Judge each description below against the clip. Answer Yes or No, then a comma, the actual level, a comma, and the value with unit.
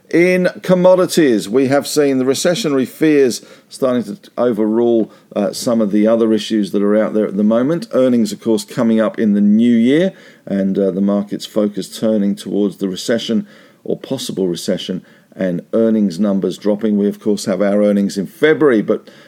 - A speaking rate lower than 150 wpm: No, average, 180 wpm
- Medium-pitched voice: No, low, 110 Hz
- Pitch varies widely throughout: Yes, wide, 5.7 semitones